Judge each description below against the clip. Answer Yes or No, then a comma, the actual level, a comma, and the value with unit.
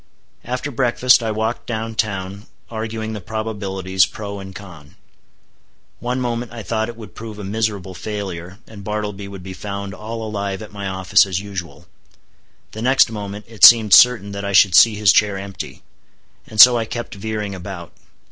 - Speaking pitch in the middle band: No, low, 105 Hz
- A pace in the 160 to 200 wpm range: Yes, average, 175 wpm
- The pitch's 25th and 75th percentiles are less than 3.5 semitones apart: Yes, narrow, 2.4 semitones